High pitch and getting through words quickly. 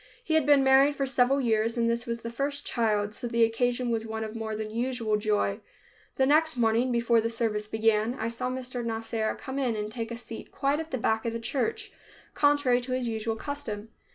Yes: high, 235 Hz; fast, 220 wpm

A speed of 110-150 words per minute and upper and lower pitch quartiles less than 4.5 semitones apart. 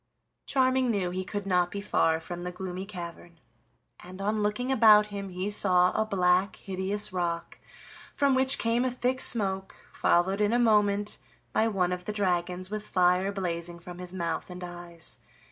No: average, 175 wpm; average, 2.8 semitones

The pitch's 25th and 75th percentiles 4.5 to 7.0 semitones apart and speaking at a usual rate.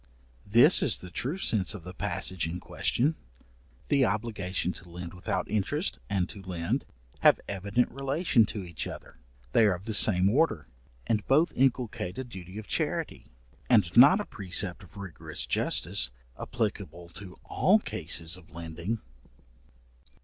Yes: average, 5.1 semitones; average, 150 wpm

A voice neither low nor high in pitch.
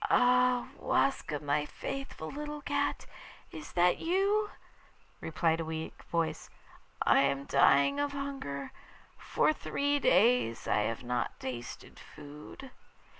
Yes: medium, 175 Hz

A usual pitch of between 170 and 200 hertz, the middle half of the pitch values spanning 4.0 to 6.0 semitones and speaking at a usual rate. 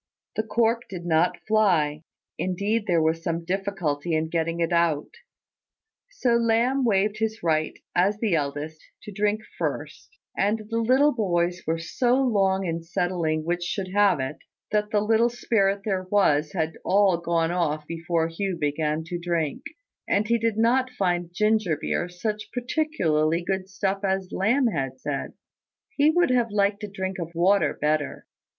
Yes: high, 190 Hz; average, 4.6 semitones; average, 160 wpm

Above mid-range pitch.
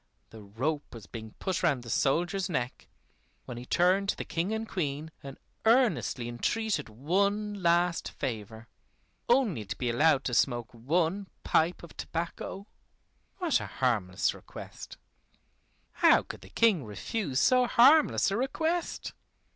No: medium, 165 Hz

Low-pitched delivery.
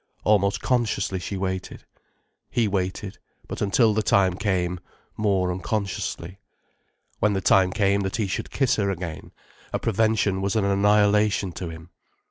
Yes: low, 100 Hz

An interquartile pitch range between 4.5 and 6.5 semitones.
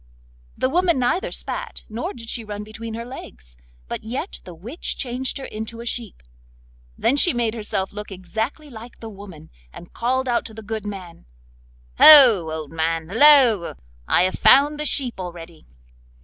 Yes: wide, 5.4 semitones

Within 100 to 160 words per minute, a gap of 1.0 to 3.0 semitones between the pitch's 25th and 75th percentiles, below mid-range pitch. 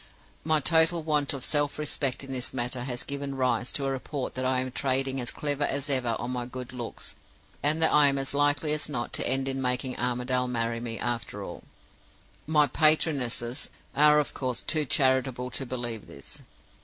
No: average, 190 wpm; narrow, 2.6 semitones; low, 130 Hz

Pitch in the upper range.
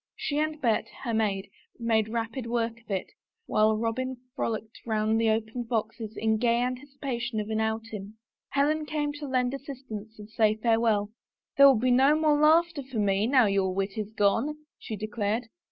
Yes: high, 230 Hz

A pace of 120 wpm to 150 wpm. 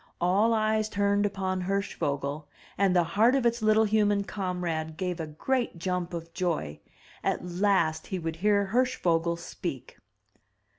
Yes: average, 145 wpm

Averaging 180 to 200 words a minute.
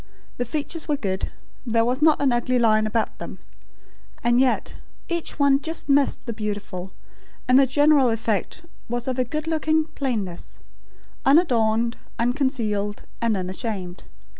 No: average, 140 wpm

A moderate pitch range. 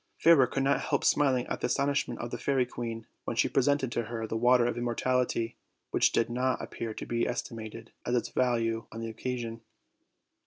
No: narrow, 1.9 semitones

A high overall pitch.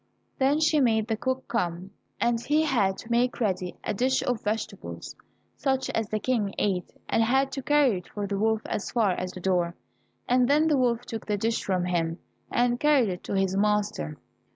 Yes: high, 225 Hz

